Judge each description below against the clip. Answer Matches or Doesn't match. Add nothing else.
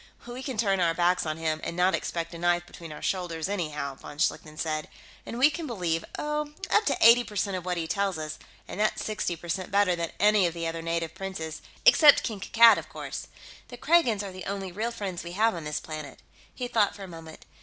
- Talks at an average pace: Doesn't match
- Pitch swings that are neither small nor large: Matches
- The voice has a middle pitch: Matches